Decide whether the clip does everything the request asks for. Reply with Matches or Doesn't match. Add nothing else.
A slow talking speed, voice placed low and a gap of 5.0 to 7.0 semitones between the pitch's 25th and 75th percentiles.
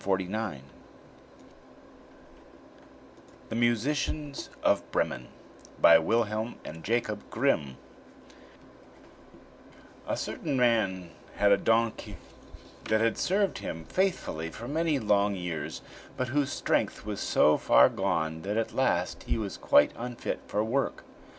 Matches